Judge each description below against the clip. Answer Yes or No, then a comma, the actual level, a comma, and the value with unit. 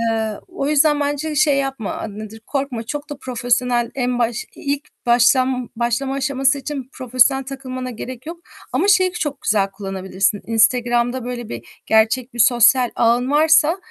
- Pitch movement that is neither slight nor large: Yes, average, 3.1 semitones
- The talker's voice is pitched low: No, very high, 255 Hz